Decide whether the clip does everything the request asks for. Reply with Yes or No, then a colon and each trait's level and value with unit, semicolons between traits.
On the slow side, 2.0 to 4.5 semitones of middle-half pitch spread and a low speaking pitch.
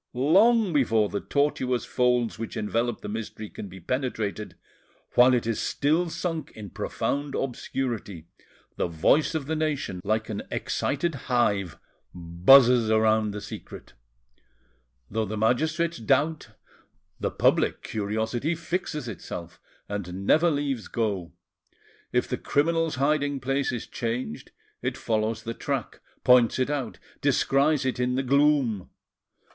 No: slow, 130 wpm; average, 4.9 semitones; low, 125 Hz